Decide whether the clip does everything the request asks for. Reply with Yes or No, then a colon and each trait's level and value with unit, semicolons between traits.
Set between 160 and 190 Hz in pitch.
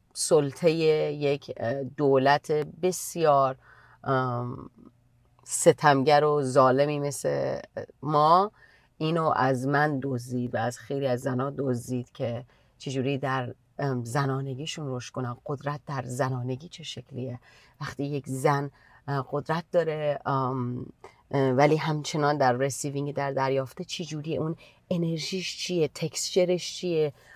No: medium, 140 Hz